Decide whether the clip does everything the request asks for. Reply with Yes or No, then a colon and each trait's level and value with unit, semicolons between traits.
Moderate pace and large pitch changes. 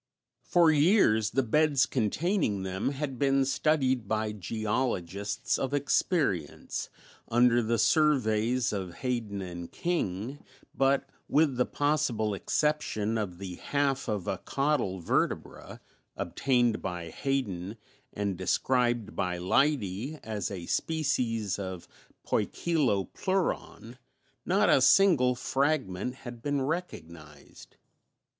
No: slow, 110 wpm; wide, 6.1 semitones